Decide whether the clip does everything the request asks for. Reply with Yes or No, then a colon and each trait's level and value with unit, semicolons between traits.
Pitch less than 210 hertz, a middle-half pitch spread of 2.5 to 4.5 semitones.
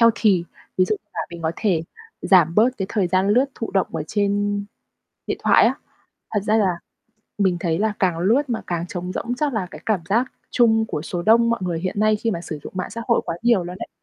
Yes: high, 200 Hz; average, 3.8 semitones